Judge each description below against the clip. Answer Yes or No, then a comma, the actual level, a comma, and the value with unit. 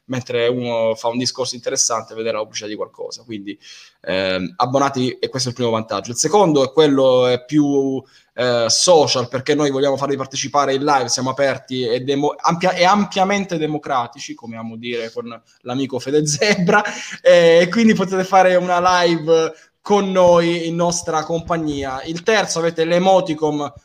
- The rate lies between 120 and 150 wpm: No, average, 160 wpm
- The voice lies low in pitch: No, medium, 145 Hz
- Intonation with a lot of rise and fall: Yes, wide, 5.7 semitones